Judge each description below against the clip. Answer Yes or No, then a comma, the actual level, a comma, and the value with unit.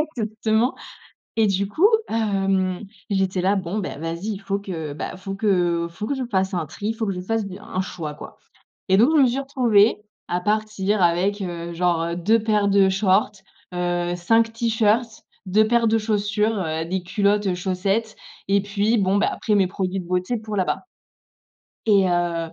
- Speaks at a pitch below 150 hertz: No, high, 200 Hz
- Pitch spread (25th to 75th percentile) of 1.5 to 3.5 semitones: Yes, average, 3.1 semitones